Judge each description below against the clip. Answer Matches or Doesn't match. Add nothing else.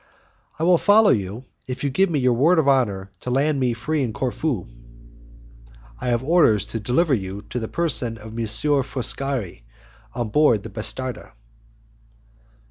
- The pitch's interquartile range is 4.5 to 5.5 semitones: Matches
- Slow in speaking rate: Doesn't match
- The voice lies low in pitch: Matches